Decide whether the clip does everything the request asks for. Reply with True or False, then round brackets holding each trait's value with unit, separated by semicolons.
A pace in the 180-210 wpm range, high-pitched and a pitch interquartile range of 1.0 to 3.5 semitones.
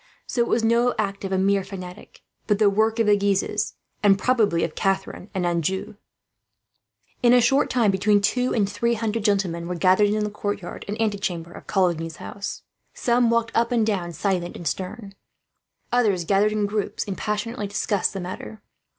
True (185 wpm; 205 Hz; 2.7 semitones)